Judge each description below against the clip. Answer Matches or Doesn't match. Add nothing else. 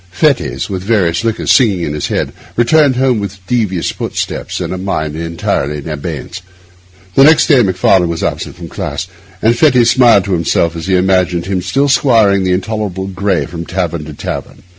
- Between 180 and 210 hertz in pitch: Doesn't match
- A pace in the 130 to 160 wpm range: Doesn't match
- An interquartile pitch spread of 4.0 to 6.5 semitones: Matches